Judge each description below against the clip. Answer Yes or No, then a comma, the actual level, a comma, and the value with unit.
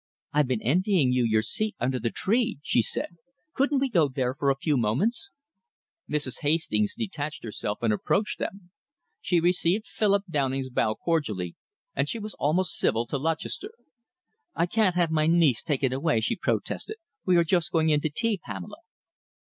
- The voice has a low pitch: No, medium, 155 Hz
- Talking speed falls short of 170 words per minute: No, average, 175 wpm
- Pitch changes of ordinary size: No, wide, 6.5 semitones